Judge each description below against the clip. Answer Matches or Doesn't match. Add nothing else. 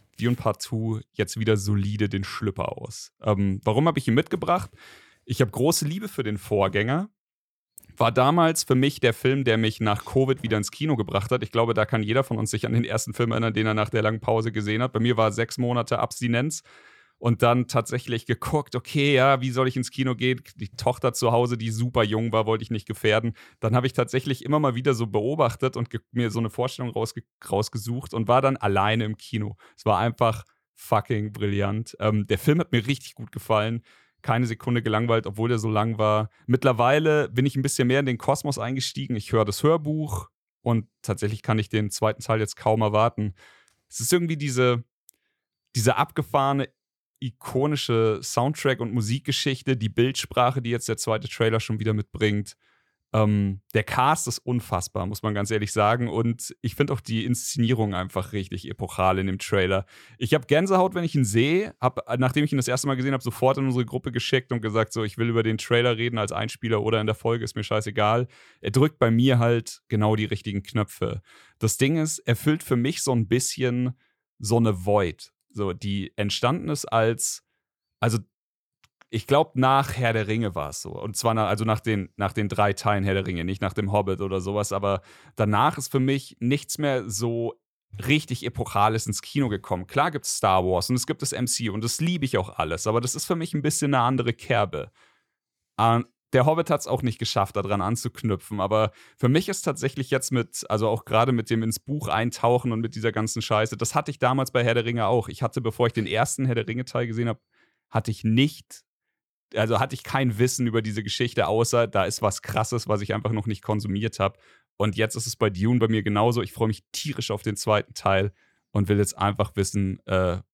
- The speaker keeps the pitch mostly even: Doesn't match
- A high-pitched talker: Doesn't match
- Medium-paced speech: Doesn't match